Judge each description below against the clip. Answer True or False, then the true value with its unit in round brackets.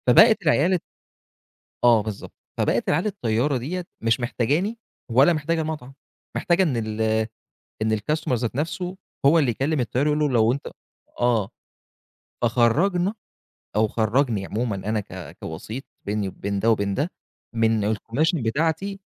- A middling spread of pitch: False (6.2 semitones)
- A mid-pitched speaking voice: False (125 Hz)